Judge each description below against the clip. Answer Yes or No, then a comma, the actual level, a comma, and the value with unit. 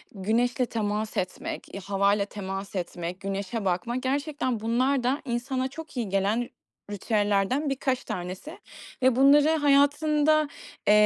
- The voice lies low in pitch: No, high, 235 Hz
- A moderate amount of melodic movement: No, wide, 5.7 semitones